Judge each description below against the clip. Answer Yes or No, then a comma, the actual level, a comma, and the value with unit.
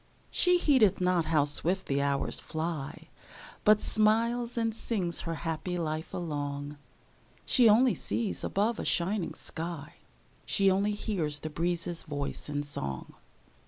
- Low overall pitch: No, medium, 175 Hz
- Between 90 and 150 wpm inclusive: Yes, slow, 135 wpm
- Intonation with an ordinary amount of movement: No, wide, 6.0 semitones